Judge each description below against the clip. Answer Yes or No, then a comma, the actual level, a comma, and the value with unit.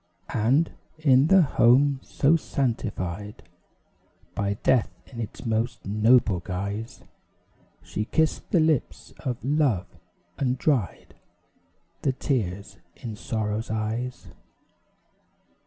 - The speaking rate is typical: No, slow, 100 wpm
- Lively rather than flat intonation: No, average, 4.6 semitones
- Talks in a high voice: No, low, 115 Hz